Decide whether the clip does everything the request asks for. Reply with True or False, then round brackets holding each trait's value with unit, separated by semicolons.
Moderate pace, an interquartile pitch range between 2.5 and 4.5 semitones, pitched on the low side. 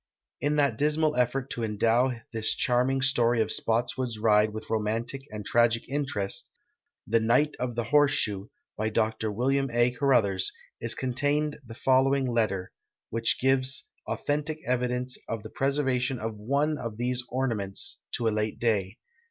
True (155 wpm; 3.4 semitones; 120 Hz)